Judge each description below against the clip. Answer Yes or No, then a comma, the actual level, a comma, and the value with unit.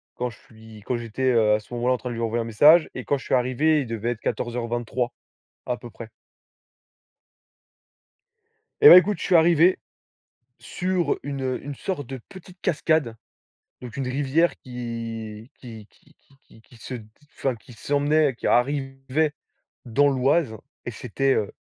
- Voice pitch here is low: Yes, low, 130 Hz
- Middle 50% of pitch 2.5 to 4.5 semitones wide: Yes, average, 3.9 semitones